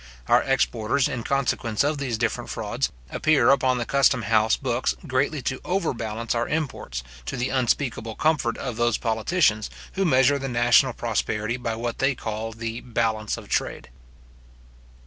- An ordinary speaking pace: Yes, average, 155 wpm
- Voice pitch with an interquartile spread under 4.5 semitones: Yes, average, 3.3 semitones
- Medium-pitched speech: No, low, 120 Hz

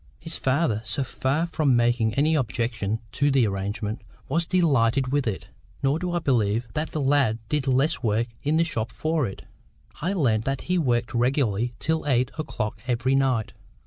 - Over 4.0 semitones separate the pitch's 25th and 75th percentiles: Yes, average, 4.7 semitones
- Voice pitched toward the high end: No, low, 130 Hz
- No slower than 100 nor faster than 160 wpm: No, average, 175 wpm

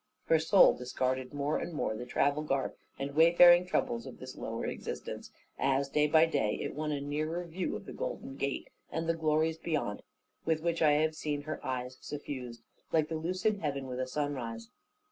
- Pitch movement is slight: No, average, 3.3 semitones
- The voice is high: No, medium, 150 Hz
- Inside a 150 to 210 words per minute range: Yes, average, 185 wpm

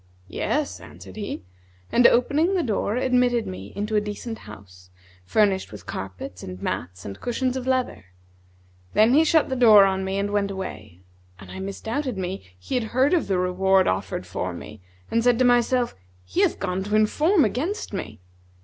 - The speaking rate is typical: Yes, average, 180 wpm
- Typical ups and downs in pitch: No, wide, 5.7 semitones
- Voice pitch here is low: No, high, 210 Hz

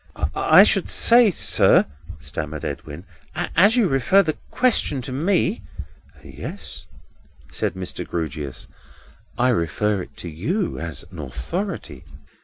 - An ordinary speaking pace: No, slow, 120 wpm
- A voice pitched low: Yes, low, 105 Hz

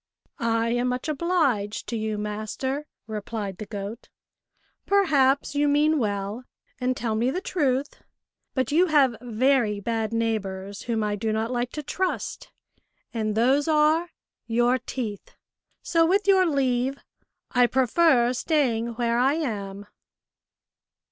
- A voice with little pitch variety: No, average, 4.7 semitones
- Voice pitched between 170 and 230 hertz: No, high, 245 Hz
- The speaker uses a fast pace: No, average, 140 wpm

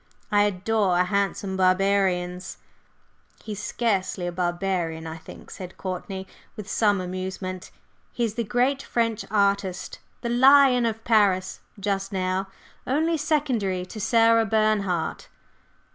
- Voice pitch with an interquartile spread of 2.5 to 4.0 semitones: Yes, average, 3.4 semitones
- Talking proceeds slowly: Yes, slow, 120 wpm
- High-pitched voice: Yes, high, 200 Hz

